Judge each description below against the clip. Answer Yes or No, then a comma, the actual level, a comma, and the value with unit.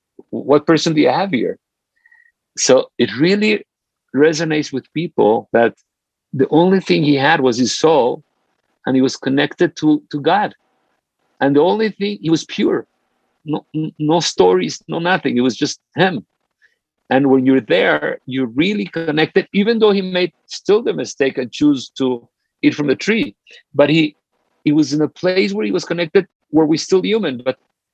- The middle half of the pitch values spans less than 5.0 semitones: No, wide, 5.5 semitones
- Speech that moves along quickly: No, average, 175 wpm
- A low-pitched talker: No, medium, 155 Hz